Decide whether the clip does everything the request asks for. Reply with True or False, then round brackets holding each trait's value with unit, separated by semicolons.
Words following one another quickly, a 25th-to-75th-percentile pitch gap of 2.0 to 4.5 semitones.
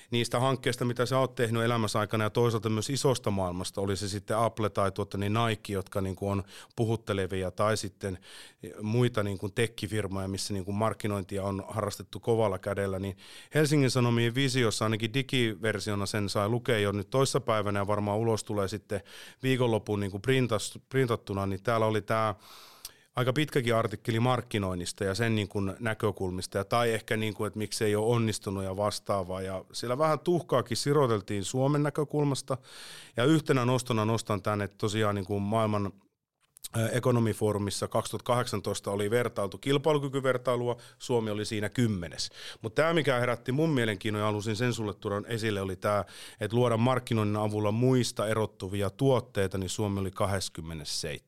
True (160 wpm; 3.1 semitones)